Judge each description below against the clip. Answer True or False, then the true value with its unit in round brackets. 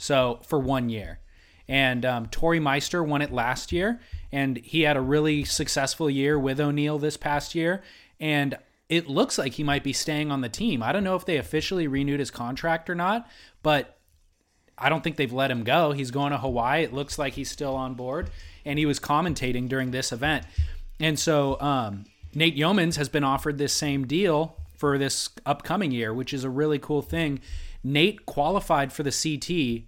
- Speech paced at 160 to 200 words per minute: True (195 wpm)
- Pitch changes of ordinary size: True (3.1 semitones)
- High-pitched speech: False (140 Hz)